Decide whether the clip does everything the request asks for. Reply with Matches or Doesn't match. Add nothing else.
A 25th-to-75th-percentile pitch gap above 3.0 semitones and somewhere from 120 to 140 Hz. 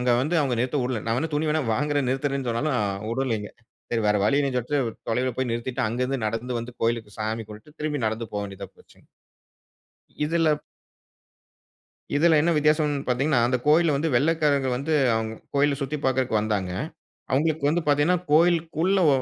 Matches